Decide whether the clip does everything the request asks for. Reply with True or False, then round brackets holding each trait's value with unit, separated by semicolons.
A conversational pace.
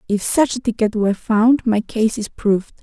False (210 wpm)